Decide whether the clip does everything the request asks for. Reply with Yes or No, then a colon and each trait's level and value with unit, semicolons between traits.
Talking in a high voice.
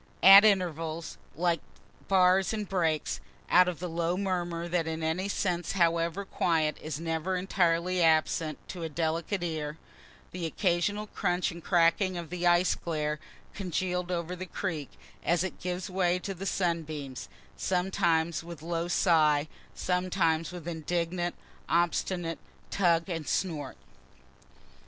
No: medium, 175 Hz